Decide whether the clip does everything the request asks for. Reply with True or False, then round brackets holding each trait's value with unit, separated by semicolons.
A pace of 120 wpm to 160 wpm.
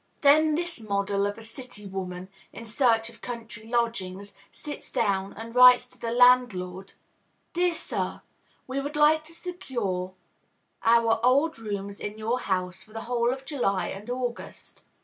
True (155 wpm)